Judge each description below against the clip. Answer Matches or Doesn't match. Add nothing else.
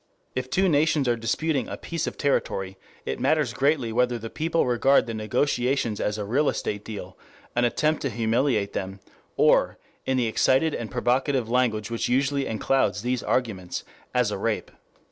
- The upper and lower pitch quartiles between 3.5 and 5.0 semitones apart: Matches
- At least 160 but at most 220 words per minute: Matches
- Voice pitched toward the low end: Matches